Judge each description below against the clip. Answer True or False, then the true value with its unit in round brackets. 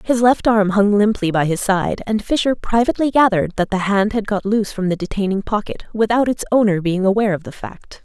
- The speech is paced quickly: True (225 wpm)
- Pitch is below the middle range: False (210 Hz)